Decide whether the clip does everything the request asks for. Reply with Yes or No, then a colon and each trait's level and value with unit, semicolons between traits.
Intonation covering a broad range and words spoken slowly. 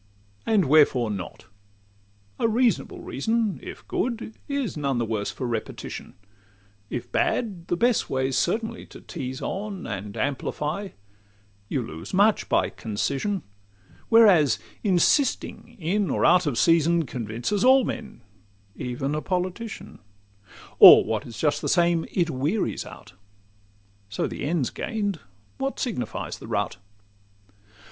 Yes: wide, 8.3 semitones; slow, 130 wpm